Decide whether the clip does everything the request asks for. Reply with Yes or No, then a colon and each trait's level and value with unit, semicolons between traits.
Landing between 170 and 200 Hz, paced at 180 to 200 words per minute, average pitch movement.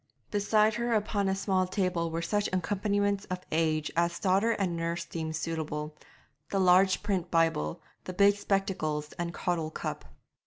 No: medium, 185 Hz; average, 155 wpm; average, 3.4 semitones